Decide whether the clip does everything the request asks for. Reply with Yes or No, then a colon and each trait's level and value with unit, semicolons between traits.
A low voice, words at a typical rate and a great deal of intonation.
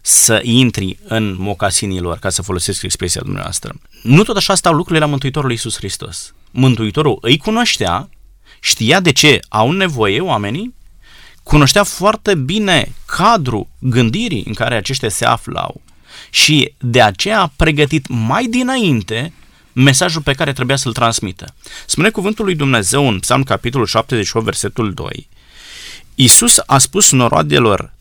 Yes: low, 130 Hz; average, 140 wpm; wide, 5.8 semitones